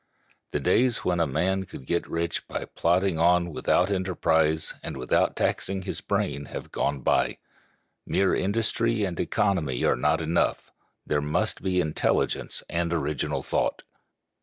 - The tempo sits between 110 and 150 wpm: Yes, average, 145 wpm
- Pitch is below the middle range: Yes, very low, 85 Hz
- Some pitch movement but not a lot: Yes, average, 3.4 semitones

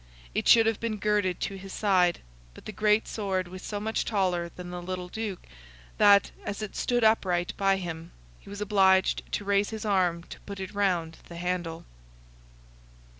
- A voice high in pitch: Yes, high, 195 Hz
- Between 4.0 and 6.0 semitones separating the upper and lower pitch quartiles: No, average, 2.7 semitones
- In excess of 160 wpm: Yes, average, 180 wpm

